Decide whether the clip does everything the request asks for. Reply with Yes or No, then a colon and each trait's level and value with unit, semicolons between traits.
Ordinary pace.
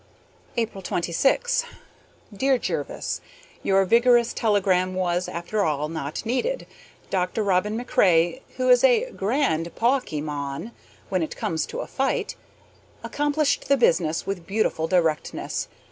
No: slow, 125 wpm